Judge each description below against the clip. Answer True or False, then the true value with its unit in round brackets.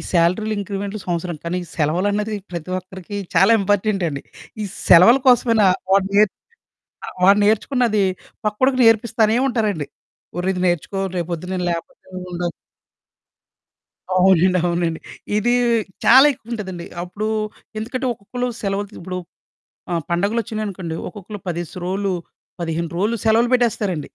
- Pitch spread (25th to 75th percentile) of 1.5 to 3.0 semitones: False (3.6 semitones)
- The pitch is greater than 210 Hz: False (195 Hz)